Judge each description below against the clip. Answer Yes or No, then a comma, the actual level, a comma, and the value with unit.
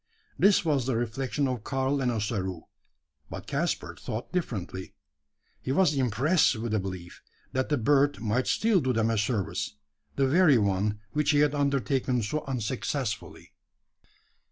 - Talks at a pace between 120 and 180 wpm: Yes, average, 150 wpm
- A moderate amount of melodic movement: Yes, average, 4.8 semitones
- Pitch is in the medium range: No, low, 130 Hz